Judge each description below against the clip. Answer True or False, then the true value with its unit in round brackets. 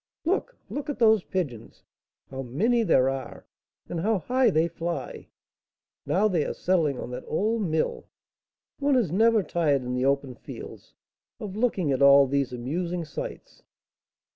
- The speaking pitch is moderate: True (170 Hz)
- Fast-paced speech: False (155 wpm)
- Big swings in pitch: True (7.8 semitones)